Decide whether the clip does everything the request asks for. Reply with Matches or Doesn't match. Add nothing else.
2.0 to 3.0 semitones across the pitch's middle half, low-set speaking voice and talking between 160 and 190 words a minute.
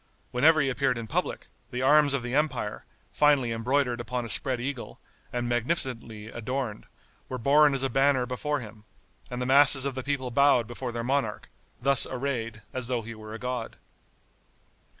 Matches